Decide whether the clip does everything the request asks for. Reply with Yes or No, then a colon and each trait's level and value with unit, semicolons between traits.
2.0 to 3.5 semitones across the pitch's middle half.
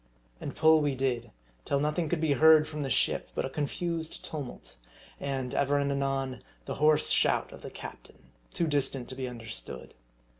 Yes: average, 2.7 semitones